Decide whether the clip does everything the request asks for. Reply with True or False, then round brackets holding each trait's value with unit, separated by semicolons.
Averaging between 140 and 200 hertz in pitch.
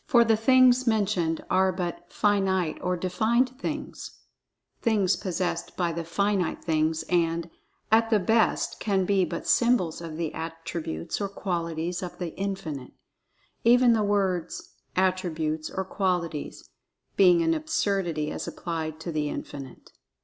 True (185 Hz)